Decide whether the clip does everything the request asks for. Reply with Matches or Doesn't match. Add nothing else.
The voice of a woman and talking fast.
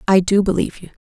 Matches